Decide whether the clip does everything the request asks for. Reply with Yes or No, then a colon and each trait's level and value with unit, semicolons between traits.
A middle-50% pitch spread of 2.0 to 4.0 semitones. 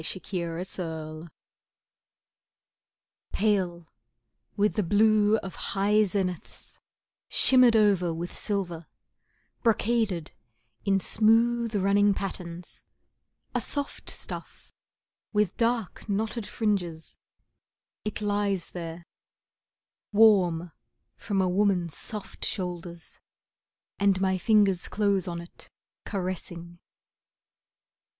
Yes: average, 3.3 semitones